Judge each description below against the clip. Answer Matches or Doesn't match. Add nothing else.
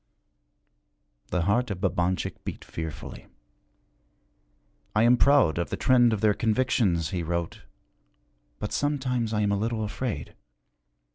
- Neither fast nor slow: Doesn't match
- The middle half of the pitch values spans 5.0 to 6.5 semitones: Matches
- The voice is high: Doesn't match